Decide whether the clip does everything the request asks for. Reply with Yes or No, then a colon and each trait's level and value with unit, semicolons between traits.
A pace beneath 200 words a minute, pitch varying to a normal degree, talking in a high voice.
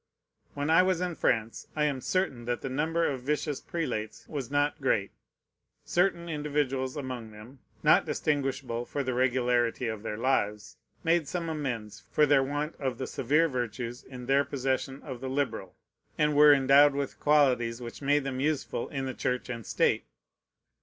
No: average, 170 wpm; average, 3.3 semitones; low, 135 Hz